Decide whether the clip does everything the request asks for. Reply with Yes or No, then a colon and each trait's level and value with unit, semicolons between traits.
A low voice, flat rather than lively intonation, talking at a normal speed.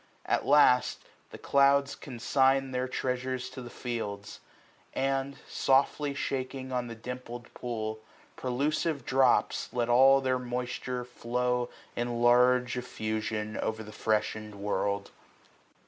No: low, 125 Hz; narrow, 2.1 semitones; slow, 115 wpm